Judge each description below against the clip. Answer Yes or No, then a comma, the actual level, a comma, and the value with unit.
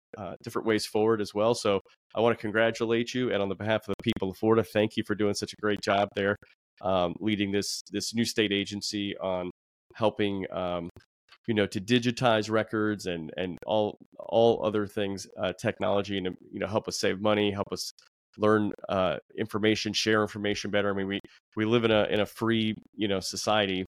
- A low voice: Yes, low, 105 Hz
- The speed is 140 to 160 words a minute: No, fast, 205 wpm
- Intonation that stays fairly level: Yes, narrow, 1.7 semitones